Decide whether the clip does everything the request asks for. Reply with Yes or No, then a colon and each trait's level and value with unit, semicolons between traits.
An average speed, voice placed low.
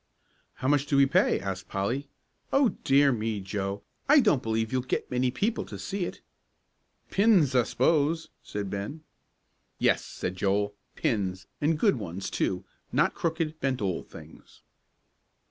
Yes: average, 150 wpm; low, 130 Hz